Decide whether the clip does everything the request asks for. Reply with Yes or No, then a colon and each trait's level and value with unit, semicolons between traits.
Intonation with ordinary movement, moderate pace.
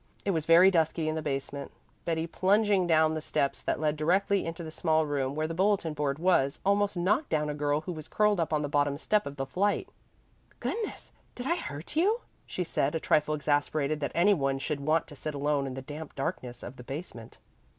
No: average, 3.9 semitones; fast, 220 wpm